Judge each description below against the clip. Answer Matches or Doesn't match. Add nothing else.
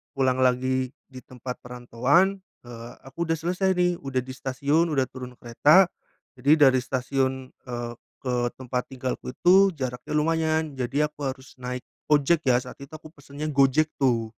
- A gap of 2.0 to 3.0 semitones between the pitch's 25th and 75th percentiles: Doesn't match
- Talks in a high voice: Doesn't match